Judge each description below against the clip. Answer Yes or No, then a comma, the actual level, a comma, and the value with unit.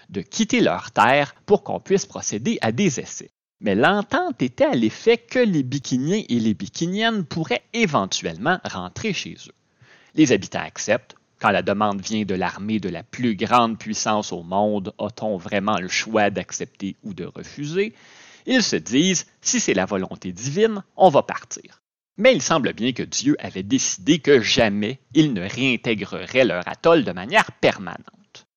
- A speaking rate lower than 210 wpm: Yes, average, 170 wpm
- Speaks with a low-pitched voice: Yes, low, 125 Hz